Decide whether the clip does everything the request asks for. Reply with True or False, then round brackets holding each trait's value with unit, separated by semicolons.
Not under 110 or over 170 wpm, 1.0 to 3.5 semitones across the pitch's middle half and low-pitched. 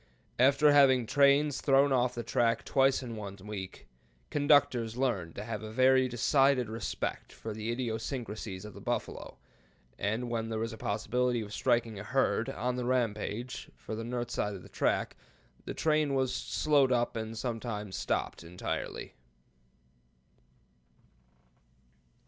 True (145 wpm; 3.2 semitones; 120 Hz)